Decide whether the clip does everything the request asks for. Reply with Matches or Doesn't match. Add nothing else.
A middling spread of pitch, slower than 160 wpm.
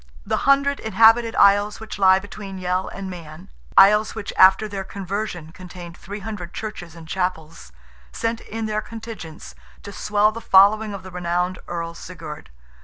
Matches